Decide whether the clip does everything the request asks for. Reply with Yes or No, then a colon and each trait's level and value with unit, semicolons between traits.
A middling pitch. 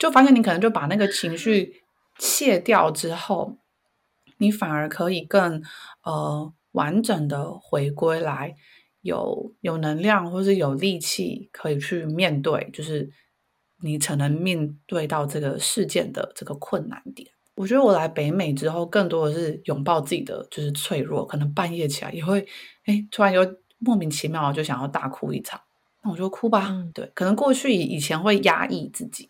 Yes: medium, 170 Hz